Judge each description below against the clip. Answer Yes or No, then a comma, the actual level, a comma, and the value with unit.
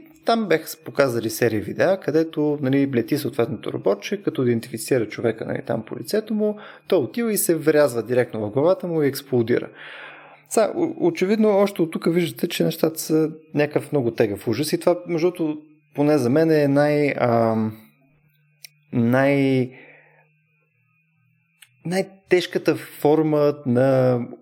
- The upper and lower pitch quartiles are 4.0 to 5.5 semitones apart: Yes, average, 4.3 semitones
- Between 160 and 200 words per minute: No, average, 140 wpm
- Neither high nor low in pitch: Yes, medium, 150 Hz